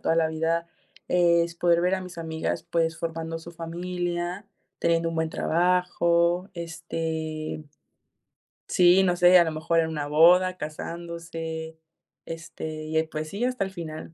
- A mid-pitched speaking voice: Yes, medium, 170 Hz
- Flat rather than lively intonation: Yes, narrow, 1.5 semitones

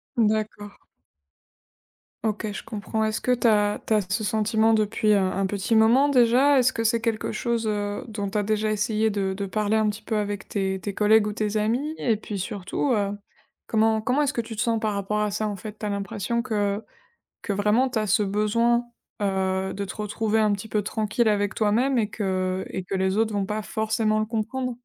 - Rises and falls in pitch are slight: Yes, narrow, 1.6 semitones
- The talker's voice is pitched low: No, high, 215 Hz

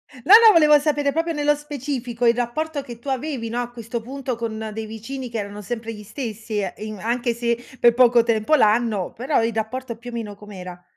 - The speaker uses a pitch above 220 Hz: Yes, high, 235 Hz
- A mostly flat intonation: No, average, 3.4 semitones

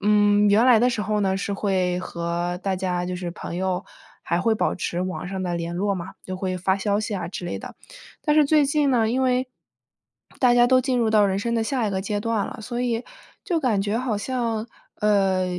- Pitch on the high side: Yes, high, 205 Hz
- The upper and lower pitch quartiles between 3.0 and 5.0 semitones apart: Yes, average, 4.2 semitones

